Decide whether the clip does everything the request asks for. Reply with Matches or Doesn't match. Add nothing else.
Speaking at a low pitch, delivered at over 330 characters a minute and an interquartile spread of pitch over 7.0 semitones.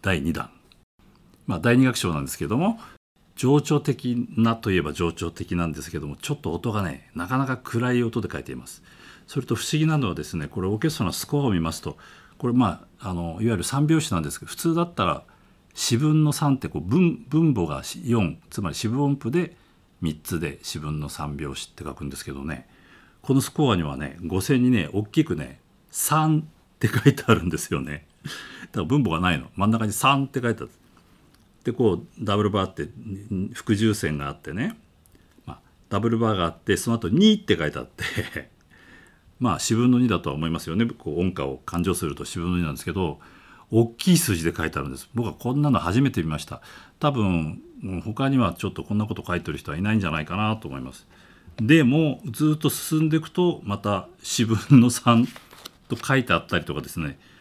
Matches